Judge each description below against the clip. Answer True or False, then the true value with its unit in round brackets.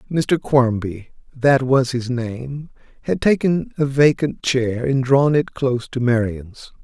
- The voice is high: False (130 Hz)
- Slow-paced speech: True (130 wpm)